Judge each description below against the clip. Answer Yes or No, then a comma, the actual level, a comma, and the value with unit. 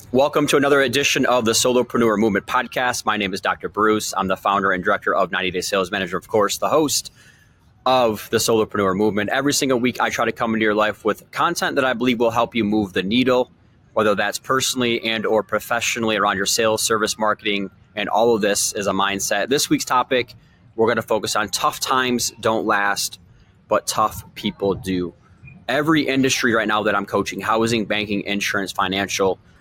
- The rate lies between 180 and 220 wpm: Yes, average, 200 wpm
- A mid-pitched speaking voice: No, low, 110 Hz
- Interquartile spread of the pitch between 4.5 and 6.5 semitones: No, average, 3.7 semitones